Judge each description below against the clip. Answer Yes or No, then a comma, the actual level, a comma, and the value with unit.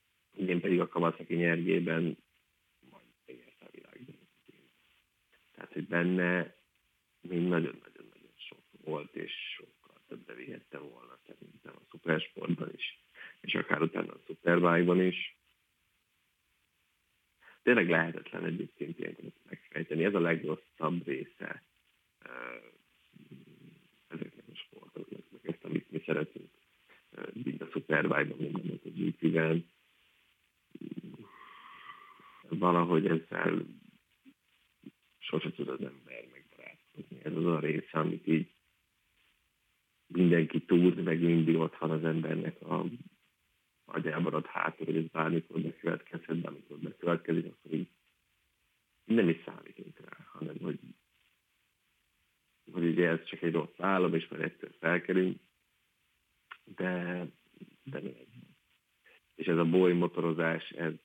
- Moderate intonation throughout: No, narrow, 1.8 semitones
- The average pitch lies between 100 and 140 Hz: No, very low, 85 Hz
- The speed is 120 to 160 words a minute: No, average, 110 wpm